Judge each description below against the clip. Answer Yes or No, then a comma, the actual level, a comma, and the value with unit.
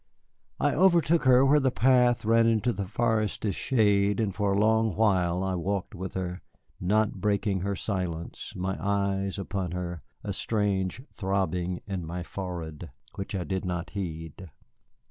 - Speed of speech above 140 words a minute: Yes, average, 155 wpm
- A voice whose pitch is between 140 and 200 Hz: No, low, 100 Hz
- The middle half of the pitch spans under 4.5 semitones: Yes, average, 3.4 semitones